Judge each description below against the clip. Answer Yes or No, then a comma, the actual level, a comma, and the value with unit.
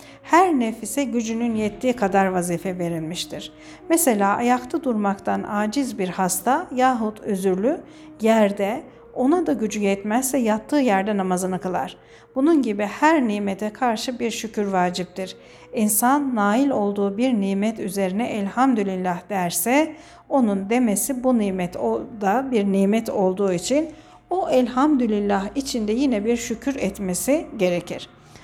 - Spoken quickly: No, average, 120 wpm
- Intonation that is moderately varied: Yes, average, 4.9 semitones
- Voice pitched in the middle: No, high, 220 Hz